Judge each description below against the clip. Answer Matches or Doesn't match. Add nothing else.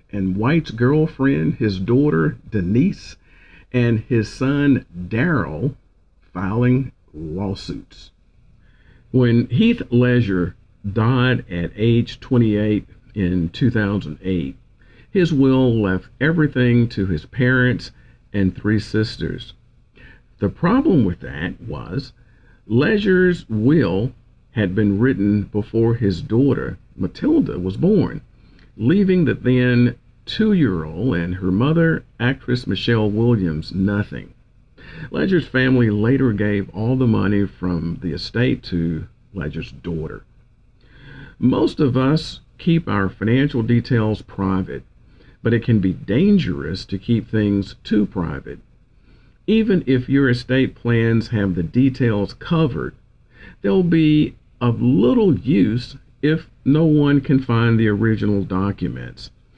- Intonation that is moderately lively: Matches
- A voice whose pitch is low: Matches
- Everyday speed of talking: Doesn't match